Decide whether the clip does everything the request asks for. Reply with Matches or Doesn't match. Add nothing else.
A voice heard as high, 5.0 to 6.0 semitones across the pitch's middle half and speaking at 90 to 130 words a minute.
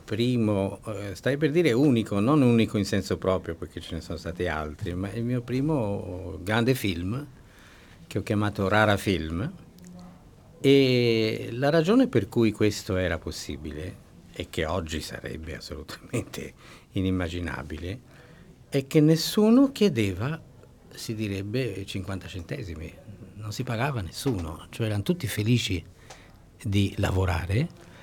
Doesn't match